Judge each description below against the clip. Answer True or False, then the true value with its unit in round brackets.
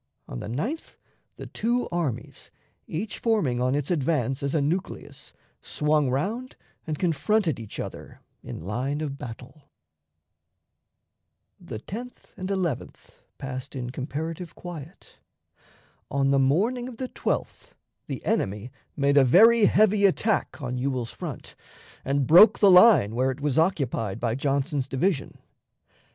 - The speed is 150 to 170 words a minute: False (135 wpm)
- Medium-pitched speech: True (145 Hz)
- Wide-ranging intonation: True (6.4 semitones)